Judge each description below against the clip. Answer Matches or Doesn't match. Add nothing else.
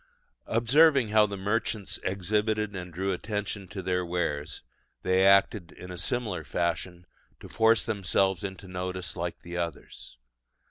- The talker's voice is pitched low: Matches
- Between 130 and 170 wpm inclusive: Matches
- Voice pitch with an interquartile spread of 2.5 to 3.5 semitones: Matches